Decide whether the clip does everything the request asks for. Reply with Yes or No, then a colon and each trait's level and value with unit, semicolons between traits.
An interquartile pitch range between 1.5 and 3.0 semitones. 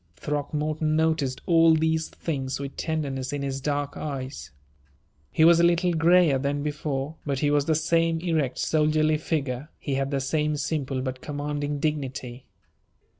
Yes: narrow, 2.5 semitones